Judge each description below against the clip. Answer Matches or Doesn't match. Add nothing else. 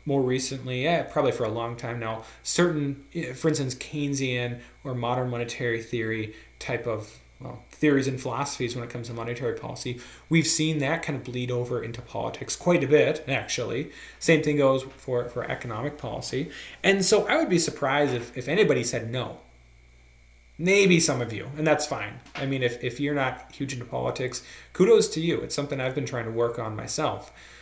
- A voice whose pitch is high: Doesn't match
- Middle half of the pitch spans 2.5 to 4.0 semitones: Matches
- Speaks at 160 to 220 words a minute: Matches